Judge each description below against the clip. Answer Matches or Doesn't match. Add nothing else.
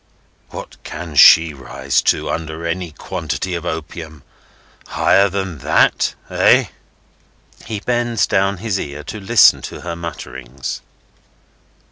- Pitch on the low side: Matches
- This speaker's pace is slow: Matches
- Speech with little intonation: Doesn't match